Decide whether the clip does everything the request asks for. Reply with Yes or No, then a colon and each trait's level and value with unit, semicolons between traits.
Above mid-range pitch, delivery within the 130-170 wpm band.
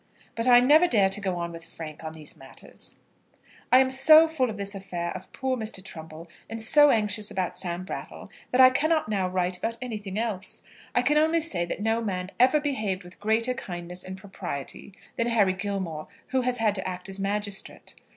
No: high, 205 Hz; average, 200 wpm